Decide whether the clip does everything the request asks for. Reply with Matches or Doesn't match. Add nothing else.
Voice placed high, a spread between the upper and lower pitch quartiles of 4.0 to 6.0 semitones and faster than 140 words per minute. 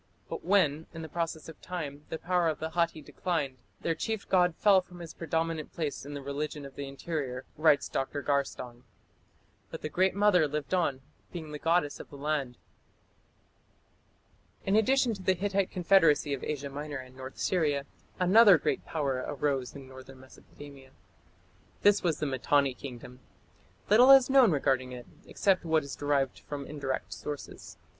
Doesn't match